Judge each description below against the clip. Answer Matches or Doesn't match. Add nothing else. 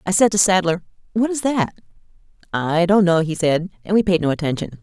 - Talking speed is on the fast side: Matches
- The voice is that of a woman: Matches